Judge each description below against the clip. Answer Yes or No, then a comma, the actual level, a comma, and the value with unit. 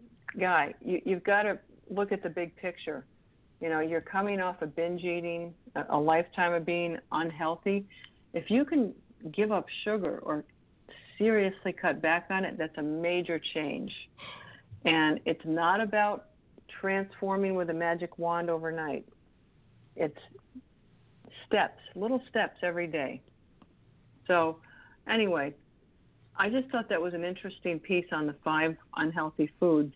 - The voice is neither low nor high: Yes, medium, 175 Hz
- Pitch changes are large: No, average, 3.3 semitones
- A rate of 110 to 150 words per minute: Yes, average, 140 wpm